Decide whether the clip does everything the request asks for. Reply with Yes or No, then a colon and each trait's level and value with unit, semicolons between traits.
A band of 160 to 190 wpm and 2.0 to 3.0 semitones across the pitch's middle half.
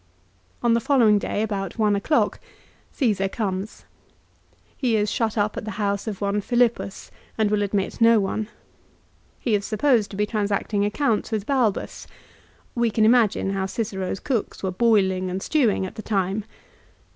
Yes: average, 165 wpm; narrow, 2.5 semitones